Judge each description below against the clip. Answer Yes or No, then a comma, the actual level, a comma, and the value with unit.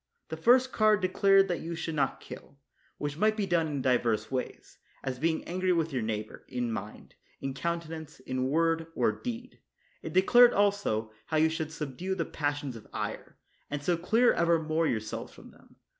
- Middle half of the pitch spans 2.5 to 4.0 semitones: No, wide, 5.4 semitones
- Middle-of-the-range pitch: Yes, medium, 160 Hz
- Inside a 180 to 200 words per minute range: Yes, average, 185 wpm